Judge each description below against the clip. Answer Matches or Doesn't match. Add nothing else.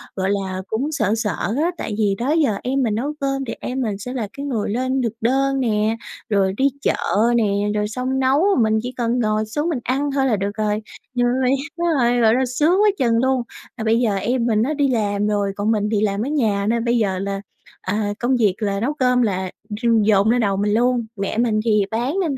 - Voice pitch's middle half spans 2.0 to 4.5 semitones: Matches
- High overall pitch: Matches